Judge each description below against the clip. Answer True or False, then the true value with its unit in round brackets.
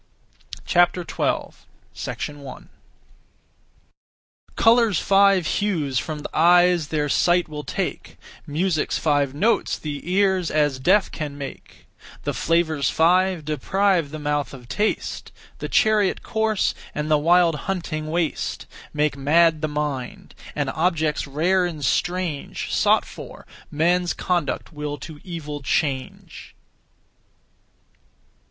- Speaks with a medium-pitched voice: True (160 Hz)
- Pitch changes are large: False (3.4 semitones)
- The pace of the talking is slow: True (115 wpm)